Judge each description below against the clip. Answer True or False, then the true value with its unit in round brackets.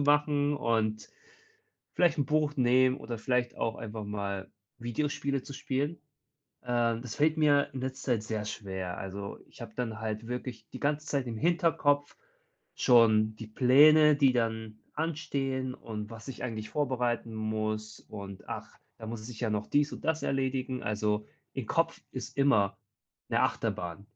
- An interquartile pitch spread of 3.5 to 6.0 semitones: True (4.6 semitones)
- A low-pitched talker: True (120 Hz)